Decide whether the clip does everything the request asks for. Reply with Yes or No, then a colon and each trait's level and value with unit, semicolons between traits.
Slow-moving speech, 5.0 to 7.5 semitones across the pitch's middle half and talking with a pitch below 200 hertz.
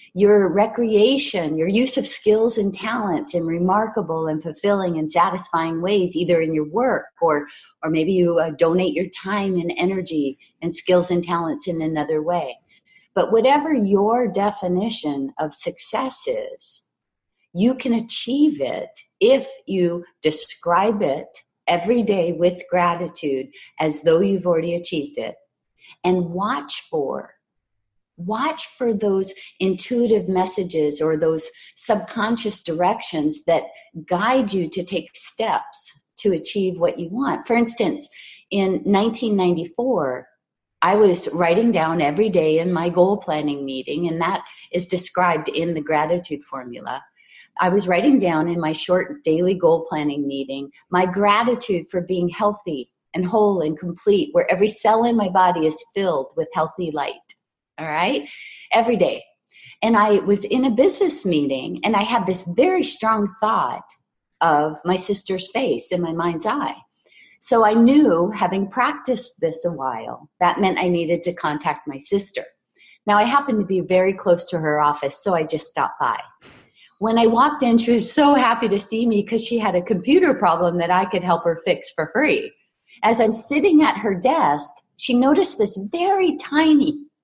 No: average, 160 wpm; average, 5.3 semitones; medium, 185 Hz